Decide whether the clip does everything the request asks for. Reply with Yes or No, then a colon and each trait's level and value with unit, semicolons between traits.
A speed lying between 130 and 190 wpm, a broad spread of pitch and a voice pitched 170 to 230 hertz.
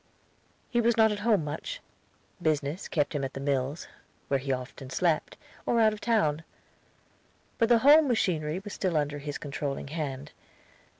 No: average, 165 wpm; wide, 7.3 semitones; medium, 155 Hz